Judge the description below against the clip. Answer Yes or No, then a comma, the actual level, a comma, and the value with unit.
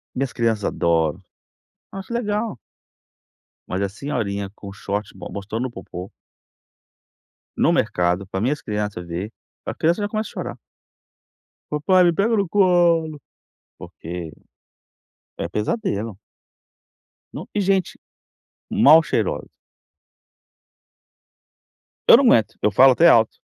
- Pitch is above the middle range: No, low, 120 Hz